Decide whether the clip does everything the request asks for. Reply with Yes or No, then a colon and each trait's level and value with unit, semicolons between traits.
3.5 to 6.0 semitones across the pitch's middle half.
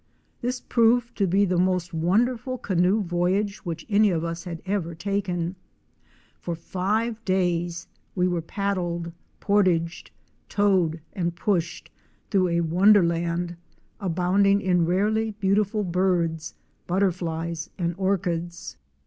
No: average, 2.9 semitones